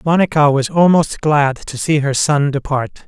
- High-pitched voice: No, medium, 145 Hz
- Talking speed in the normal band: Yes, average, 175 wpm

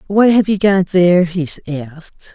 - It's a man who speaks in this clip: No, female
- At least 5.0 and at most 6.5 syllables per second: No, 4.5 syllables/s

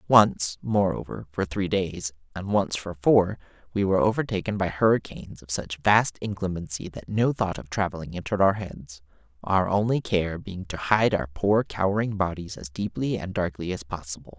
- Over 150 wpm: Yes, average, 175 wpm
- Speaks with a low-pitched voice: Yes, very low, 95 Hz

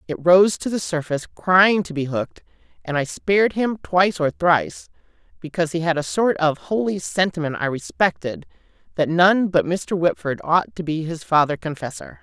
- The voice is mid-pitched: Yes, medium, 170 Hz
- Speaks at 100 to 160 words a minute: No, average, 180 wpm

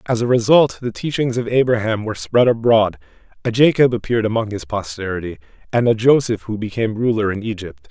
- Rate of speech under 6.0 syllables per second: No, 6.1 syllables/s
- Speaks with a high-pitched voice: No, low, 115 Hz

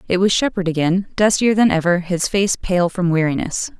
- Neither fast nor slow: Yes, average, 190 wpm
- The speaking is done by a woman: Yes, female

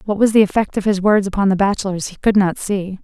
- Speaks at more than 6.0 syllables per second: Yes, 6.3 syllables/s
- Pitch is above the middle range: Yes, high, 200 Hz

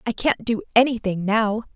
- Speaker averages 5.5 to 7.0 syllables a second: No, 5.0 syllables/s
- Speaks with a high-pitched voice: Yes, high, 225 Hz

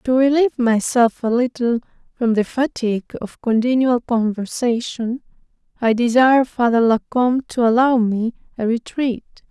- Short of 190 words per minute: Yes, slow, 135 wpm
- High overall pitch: Yes, high, 240 Hz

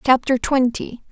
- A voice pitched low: No, very high, 255 Hz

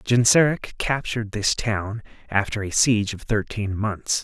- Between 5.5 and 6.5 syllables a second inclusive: No, 4.5 syllables/s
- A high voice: No, low, 110 Hz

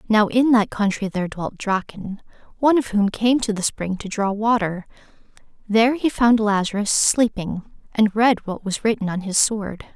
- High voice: Yes, high, 215 Hz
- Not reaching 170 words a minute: No, average, 180 wpm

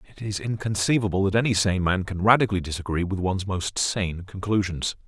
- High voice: No, low, 100 Hz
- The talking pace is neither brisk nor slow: Yes, average, 175 wpm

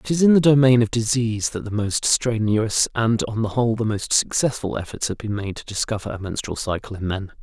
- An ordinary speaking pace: No, fast, 235 wpm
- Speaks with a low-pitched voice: Yes, low, 110 Hz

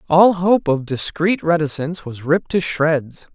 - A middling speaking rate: Yes, average, 160 wpm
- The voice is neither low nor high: Yes, medium, 165 Hz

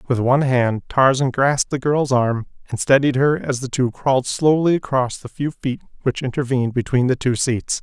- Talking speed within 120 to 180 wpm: No, average, 200 wpm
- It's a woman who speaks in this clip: No, male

